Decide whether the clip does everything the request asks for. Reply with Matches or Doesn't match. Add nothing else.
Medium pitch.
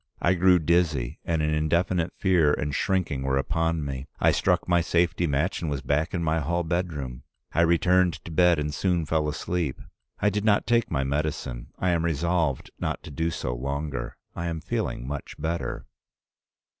Doesn't match